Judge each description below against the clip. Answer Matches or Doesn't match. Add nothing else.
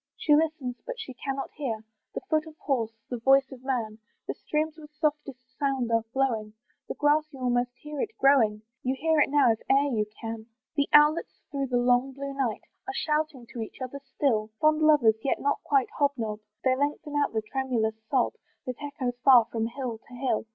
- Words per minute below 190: Doesn't match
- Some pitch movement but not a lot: Matches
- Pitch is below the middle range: Doesn't match